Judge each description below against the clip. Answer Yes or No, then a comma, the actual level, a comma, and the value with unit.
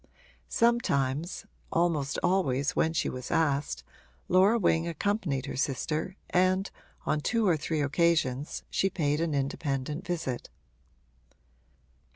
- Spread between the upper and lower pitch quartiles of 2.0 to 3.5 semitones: No, average, 4.6 semitones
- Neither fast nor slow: No, slow, 115 wpm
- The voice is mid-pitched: Yes, medium, 160 Hz